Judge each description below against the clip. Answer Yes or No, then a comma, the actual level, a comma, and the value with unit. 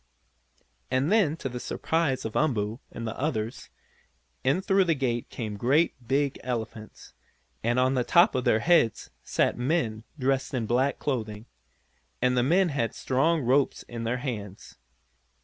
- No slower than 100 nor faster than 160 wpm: Yes, average, 155 wpm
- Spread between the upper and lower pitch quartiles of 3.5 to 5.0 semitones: Yes, average, 3.9 semitones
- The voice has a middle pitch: No, low, 130 Hz